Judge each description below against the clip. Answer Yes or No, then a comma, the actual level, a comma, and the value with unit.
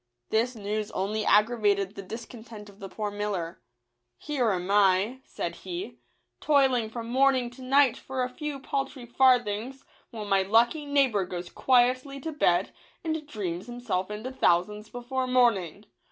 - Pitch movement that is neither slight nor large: Yes, average, 4.3 semitones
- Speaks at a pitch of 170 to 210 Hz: No, high, 230 Hz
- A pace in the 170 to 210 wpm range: No, average, 155 wpm